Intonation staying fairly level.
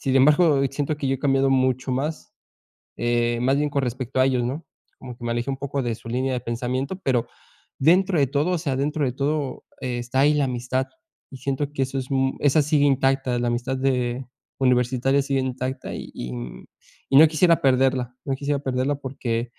Yes: narrow, 2.1 semitones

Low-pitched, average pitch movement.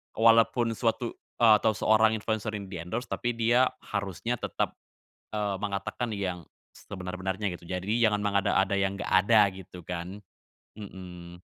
Yes: low, 100 Hz; average, 3.0 semitones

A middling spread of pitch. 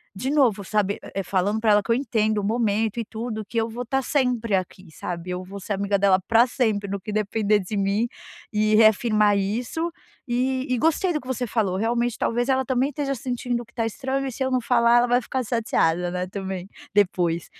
Yes: average, 3.6 semitones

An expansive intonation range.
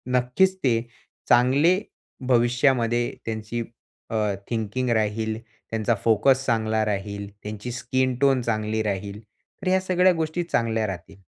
No: average, 3.2 semitones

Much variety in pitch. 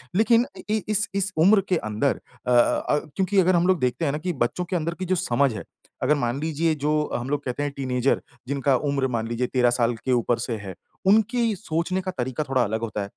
Yes: wide, 6.8 semitones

